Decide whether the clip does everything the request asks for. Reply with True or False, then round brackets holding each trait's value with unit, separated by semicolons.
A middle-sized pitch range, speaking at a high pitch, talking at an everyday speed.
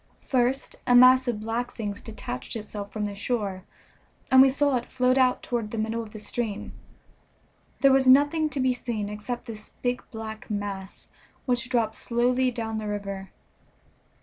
True (3.2 semitones; 235 Hz; 170 wpm)